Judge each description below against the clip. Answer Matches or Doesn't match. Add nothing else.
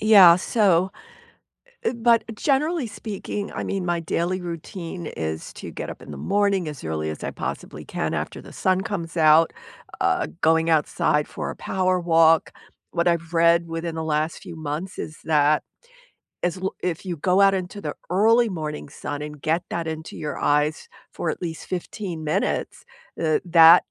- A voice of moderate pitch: Matches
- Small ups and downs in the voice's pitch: Doesn't match